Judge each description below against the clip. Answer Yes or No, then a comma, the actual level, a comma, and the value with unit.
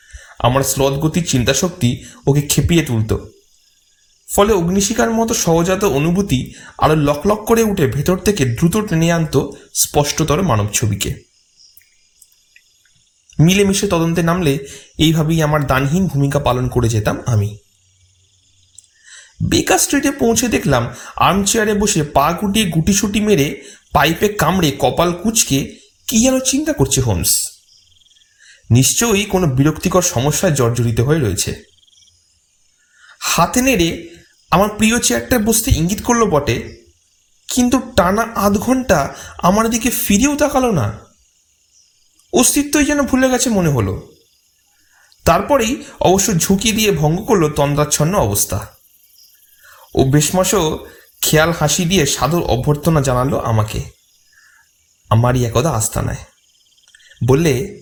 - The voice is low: No, medium, 155 Hz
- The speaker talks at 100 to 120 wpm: Yes, average, 115 wpm